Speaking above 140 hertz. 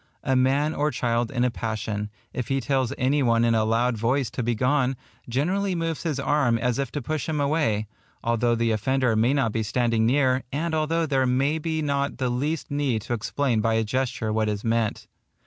No: low, 125 Hz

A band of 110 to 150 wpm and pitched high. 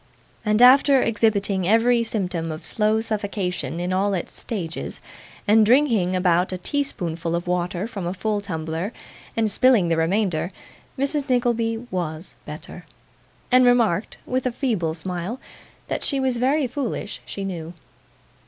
Yes: average, 145 wpm; high, 205 Hz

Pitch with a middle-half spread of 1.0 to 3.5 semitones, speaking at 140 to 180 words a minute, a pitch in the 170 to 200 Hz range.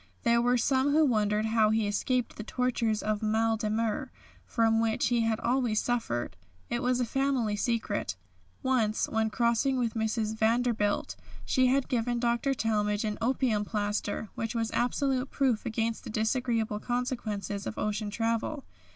No: narrow, 2.4 semitones; average, 160 wpm; high, 225 Hz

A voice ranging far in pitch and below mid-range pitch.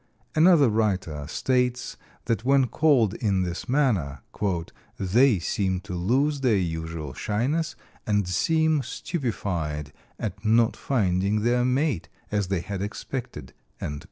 Yes: wide, 6.1 semitones; low, 105 Hz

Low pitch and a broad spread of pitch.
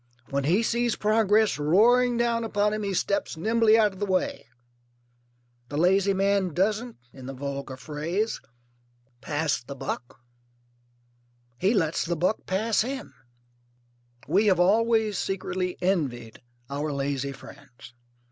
No: high, 190 Hz; wide, 6.7 semitones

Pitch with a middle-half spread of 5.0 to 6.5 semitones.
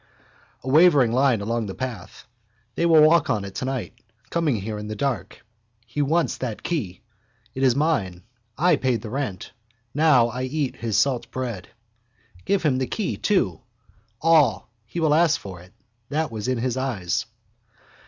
Yes: wide, 5.5 semitones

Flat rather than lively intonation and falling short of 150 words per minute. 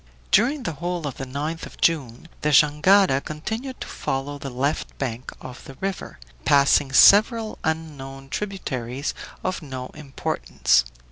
No: average, 5.0 semitones; average, 140 wpm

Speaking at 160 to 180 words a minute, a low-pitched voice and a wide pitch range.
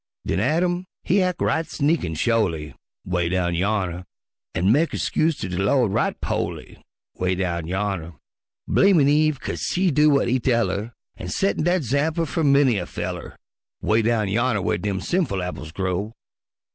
Yes: average, 170 wpm; low, 115 Hz; wide, 8.8 semitones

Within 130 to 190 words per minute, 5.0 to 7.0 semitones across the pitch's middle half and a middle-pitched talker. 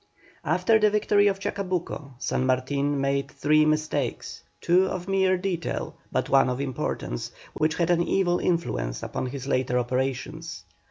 Yes: average, 150 wpm; wide, 5.4 semitones; medium, 155 Hz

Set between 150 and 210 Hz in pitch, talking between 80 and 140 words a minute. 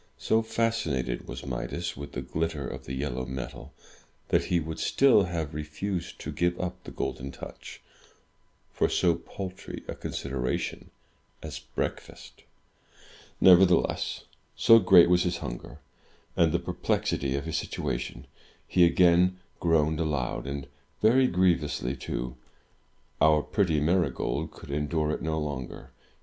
No: very low, 80 Hz; slow, 135 wpm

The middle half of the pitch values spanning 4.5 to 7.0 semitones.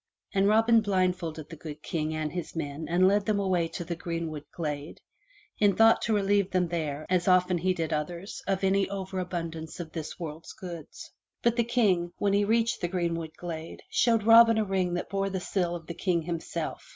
No: average, 3.3 semitones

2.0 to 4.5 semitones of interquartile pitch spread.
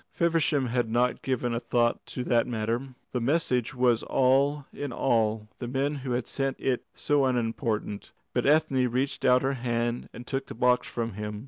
Yes: narrow, 2.4 semitones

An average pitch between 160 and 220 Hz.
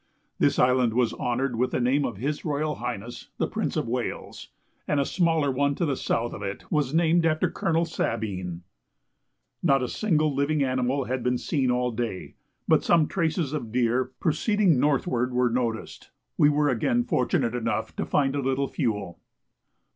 No: low, 130 Hz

